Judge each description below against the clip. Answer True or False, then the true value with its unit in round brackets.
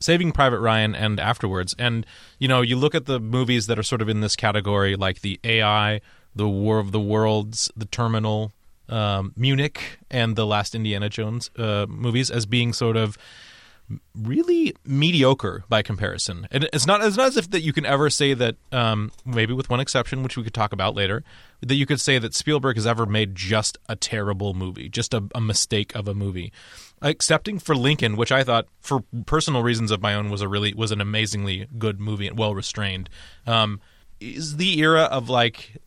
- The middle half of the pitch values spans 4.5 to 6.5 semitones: False (3.8 semitones)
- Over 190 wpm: True (200 wpm)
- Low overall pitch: True (110 Hz)